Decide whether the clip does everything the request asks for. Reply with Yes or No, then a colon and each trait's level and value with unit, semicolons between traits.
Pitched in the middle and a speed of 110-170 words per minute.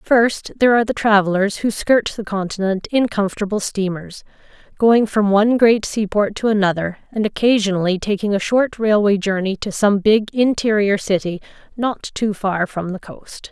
No: high, 205 Hz; average, 165 wpm